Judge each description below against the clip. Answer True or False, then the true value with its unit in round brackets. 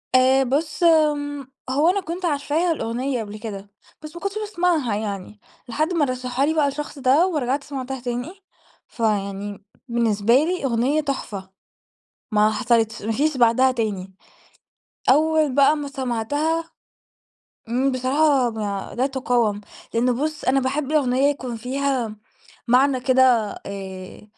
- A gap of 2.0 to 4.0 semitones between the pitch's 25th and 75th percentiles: False (4.4 semitones)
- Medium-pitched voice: False (260 Hz)